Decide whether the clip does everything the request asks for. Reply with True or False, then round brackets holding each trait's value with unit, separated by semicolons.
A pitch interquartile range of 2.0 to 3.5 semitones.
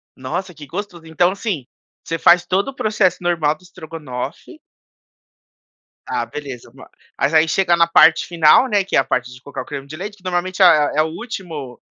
False (3.9 semitones)